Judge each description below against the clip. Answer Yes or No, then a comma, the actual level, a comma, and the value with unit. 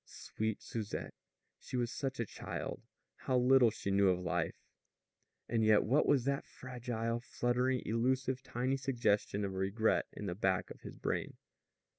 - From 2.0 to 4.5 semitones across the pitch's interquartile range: Yes, average, 3.8 semitones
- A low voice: Yes, low, 115 Hz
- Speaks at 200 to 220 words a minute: No, average, 160 wpm